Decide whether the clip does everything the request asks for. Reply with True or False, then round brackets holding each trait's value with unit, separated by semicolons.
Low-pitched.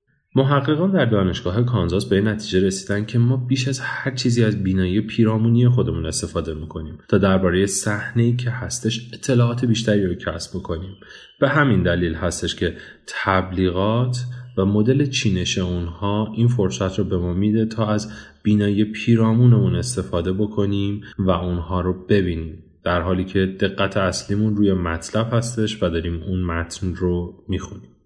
True (100 Hz)